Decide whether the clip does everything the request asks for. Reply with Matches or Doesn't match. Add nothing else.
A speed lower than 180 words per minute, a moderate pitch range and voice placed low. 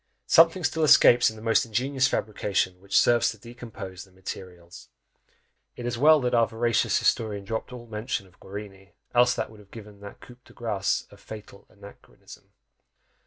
Matches